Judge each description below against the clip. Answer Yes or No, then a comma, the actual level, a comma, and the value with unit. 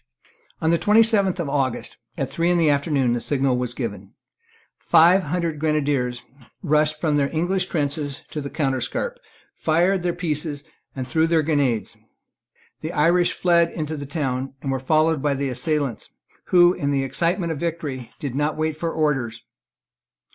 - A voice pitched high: No, medium, 150 Hz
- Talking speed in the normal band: Yes, average, 165 wpm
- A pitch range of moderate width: Yes, average, 3.7 semitones